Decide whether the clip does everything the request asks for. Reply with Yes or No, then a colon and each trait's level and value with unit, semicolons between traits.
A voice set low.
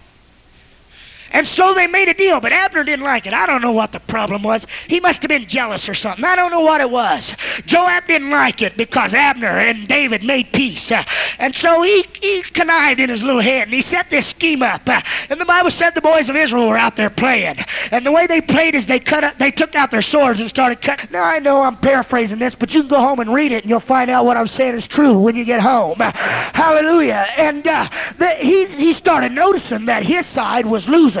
No: very high, 275 Hz